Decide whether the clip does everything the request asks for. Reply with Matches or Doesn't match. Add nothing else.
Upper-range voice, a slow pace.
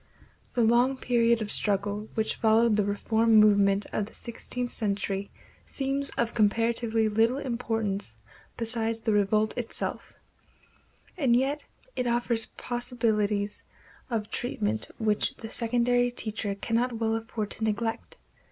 Matches